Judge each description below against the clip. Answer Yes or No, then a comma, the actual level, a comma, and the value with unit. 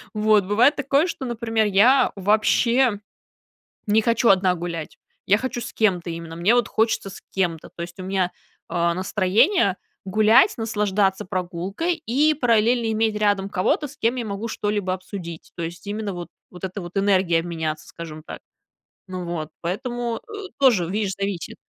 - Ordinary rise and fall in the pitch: Yes, average, 4.0 semitones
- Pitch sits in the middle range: No, high, 205 Hz